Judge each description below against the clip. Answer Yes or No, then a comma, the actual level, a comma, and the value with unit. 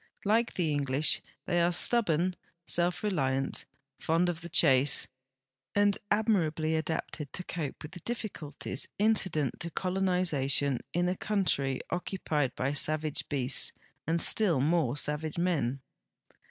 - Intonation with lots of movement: No, average, 4.0 semitones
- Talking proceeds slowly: Yes, slow, 125 wpm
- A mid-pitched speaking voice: Yes, medium, 160 Hz